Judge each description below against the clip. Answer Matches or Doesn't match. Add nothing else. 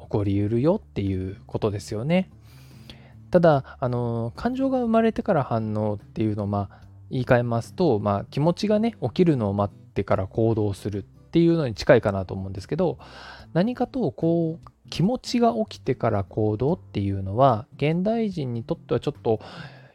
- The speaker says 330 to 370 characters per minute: Matches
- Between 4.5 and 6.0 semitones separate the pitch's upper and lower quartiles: Doesn't match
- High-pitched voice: Doesn't match